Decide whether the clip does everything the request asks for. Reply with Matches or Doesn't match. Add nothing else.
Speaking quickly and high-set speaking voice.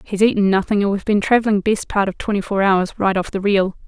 Matches